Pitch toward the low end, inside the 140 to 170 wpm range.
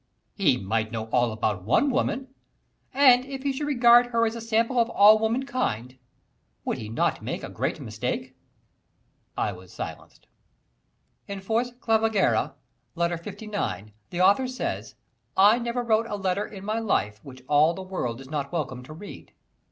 No: high, 200 Hz; average, 165 wpm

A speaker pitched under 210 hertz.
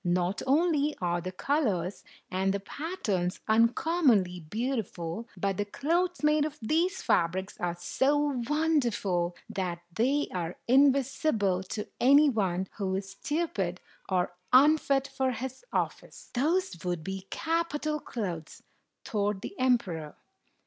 No: high, 225 Hz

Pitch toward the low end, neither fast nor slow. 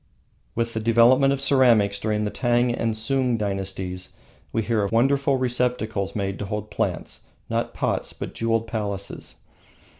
Yes: low, 115 Hz; average, 150 wpm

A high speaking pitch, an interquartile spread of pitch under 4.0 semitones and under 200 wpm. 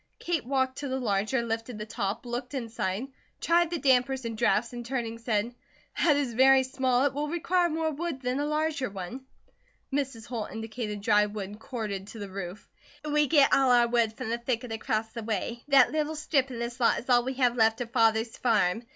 No: high, 240 Hz; average, 3.3 semitones; fast, 205 wpm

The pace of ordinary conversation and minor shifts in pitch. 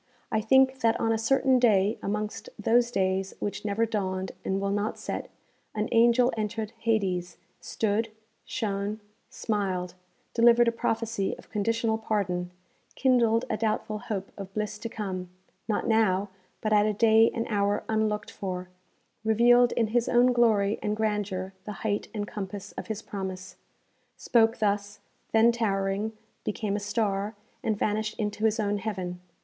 Yes: average, 155 wpm; narrow, 2.2 semitones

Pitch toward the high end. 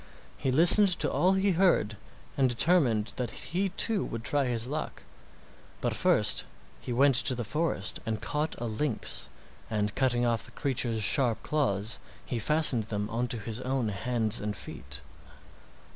No: low, 120 Hz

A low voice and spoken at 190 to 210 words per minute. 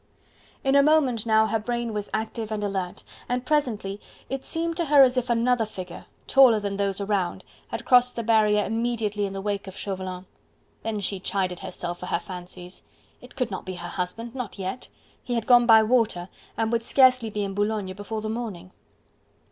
No: high, 215 Hz; average, 195 wpm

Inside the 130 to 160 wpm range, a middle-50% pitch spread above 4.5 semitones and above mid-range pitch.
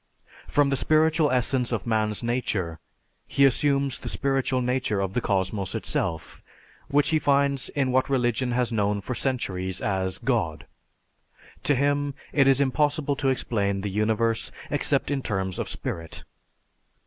No: average, 150 wpm; wide, 5.4 semitones; low, 125 Hz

